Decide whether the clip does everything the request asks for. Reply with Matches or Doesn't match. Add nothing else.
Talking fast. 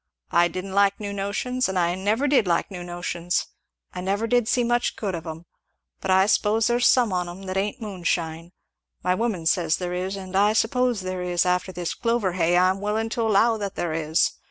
Matches